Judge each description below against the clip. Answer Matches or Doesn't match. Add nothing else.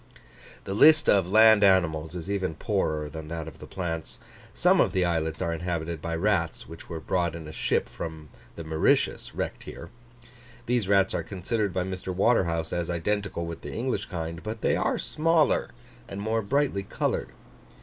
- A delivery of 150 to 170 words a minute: Doesn't match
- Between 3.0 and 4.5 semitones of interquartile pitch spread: Matches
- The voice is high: Doesn't match